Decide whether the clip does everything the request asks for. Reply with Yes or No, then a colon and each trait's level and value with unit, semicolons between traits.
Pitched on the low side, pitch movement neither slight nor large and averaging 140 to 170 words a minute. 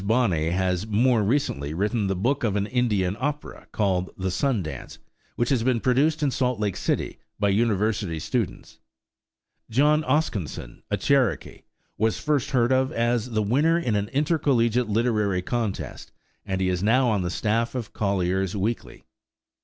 Yes: low, 110 Hz; average, 4.6 semitones; average, 160 wpm